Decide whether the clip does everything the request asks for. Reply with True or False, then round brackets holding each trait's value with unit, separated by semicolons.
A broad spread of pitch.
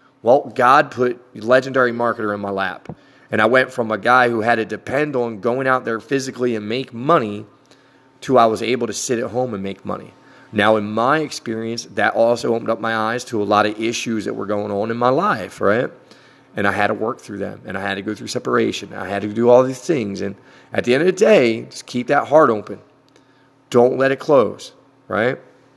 False (3.3 semitones)